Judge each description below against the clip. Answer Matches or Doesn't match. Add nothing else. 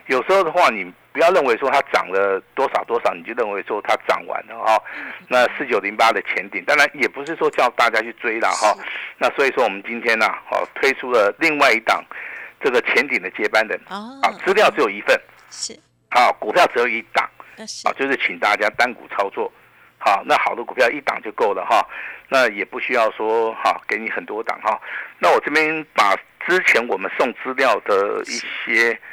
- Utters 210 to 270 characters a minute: Doesn't match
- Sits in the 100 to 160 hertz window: Doesn't match